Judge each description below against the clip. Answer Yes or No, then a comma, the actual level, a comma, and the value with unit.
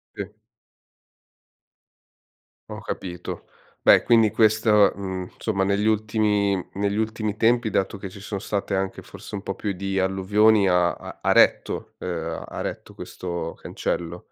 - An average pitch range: No, narrow, 2.2 semitones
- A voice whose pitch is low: Yes, low, 100 Hz